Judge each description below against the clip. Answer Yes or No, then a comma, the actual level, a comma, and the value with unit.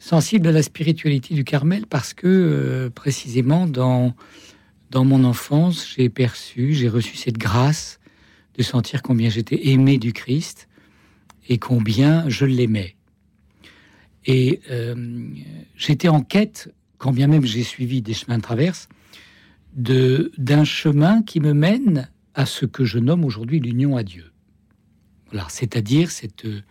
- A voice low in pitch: Yes, low, 130 Hz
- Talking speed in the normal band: No, slow, 140 wpm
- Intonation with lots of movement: No, average, 4.9 semitones